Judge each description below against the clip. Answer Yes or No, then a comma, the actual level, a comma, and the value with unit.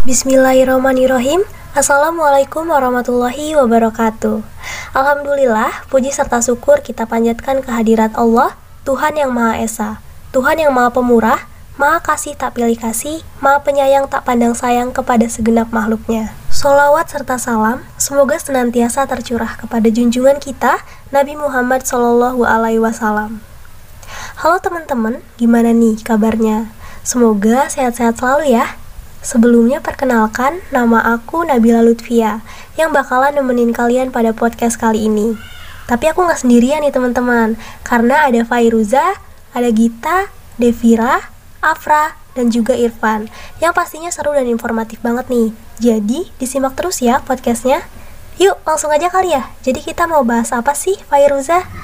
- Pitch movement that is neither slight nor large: Yes, average, 3.5 semitones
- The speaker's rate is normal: Yes, average, 125 wpm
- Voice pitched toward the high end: Yes, very high, 250 Hz